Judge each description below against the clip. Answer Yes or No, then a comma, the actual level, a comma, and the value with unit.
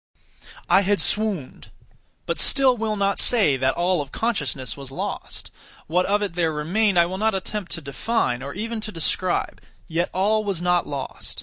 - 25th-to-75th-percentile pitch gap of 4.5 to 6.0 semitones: Yes, wide, 5.5 semitones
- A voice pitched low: No, medium, 185 Hz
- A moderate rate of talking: Yes, average, 180 wpm